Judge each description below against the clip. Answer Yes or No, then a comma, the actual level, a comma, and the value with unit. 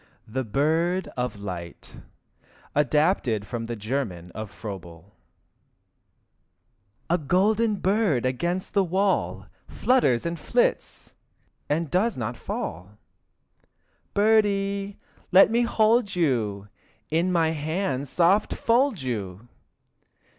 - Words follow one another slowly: Yes, slow, 105 wpm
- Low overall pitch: No, medium, 160 Hz